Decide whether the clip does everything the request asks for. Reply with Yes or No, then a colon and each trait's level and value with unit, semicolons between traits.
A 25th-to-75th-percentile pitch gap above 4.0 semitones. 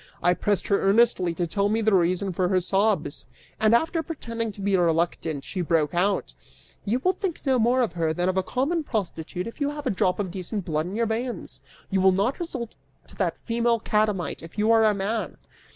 Yes: average, 4.5 semitones